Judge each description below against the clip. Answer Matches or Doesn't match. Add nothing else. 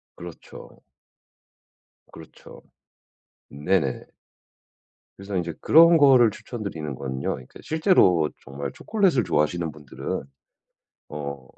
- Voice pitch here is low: Matches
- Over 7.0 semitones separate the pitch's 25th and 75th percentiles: Matches